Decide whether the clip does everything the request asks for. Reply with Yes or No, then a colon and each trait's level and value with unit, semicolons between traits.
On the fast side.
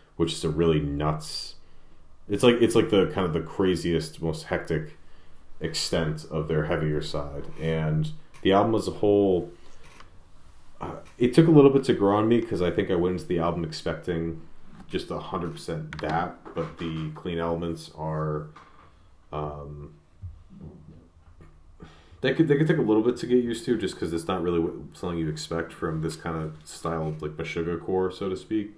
No: average, 190 wpm